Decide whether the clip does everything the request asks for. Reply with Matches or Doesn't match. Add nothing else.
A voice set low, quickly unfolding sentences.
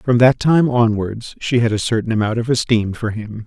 Matches